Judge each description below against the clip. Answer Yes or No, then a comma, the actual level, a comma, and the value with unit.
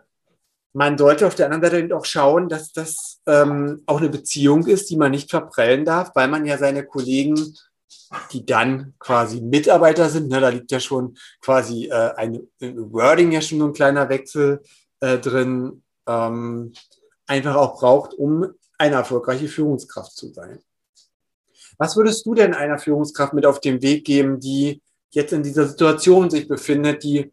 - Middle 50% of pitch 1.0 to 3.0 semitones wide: Yes, narrow, 2.5 semitones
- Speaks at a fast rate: No, average, 170 wpm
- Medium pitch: Yes, medium, 145 Hz